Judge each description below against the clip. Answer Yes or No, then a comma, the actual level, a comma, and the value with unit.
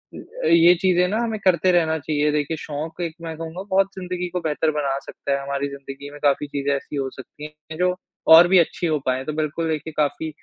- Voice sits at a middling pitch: Yes, medium, 160 Hz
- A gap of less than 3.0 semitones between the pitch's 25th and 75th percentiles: No, average, 3.3 semitones